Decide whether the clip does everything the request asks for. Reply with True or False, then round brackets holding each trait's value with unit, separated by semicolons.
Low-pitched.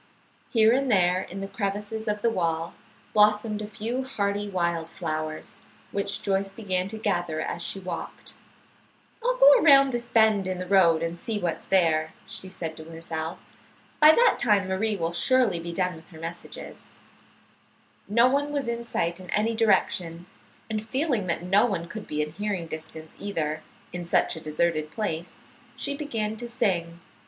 False (195 Hz)